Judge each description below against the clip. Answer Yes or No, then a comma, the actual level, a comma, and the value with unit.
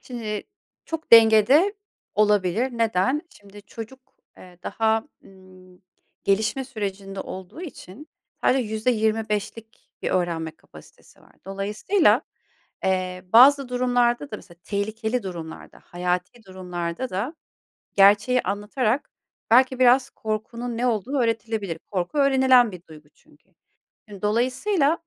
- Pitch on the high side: Yes, high, 220 Hz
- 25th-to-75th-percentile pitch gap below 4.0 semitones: No, average, 4.8 semitones